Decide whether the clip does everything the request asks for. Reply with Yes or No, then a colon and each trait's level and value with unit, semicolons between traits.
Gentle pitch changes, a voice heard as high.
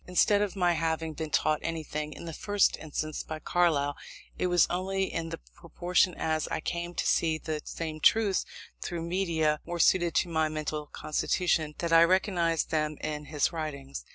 No: narrow, 2.3 semitones; medium, 165 Hz